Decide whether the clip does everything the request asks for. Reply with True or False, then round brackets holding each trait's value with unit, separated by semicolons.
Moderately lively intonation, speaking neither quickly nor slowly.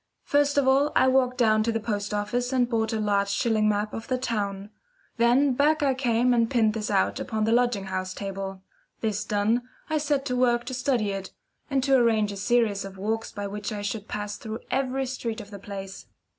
False (3.5 semitones; 220 wpm)